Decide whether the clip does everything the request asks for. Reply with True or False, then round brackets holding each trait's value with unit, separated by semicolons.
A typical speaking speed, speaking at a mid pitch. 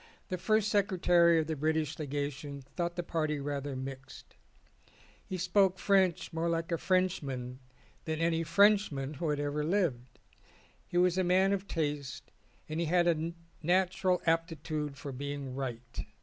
True (150 wpm; 165 Hz)